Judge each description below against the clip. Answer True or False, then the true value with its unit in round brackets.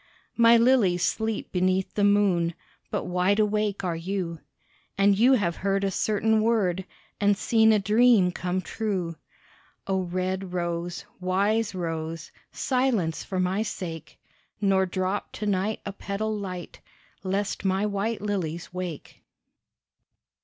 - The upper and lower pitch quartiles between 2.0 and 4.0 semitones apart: True (2.7 semitones)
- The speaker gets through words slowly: True (130 wpm)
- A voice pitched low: False (195 Hz)